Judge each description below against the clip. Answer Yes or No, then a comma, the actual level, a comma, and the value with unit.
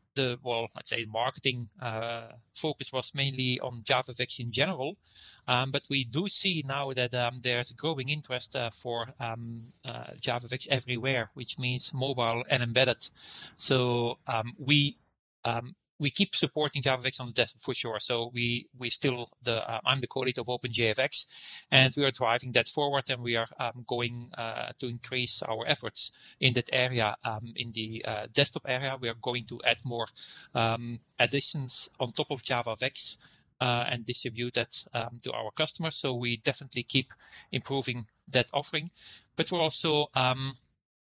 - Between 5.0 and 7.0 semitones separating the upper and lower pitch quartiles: No, narrow, 2.6 semitones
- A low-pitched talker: Yes, low, 125 Hz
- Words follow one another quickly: No, average, 170 wpm